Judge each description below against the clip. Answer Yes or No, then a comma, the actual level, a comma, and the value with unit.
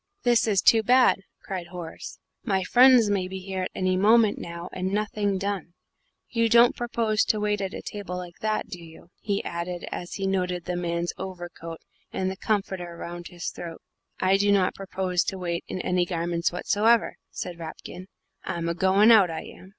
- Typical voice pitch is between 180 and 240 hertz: Yes, medium, 185 Hz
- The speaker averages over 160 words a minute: Yes, average, 185 wpm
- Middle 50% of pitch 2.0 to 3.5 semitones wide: Yes, average, 2.9 semitones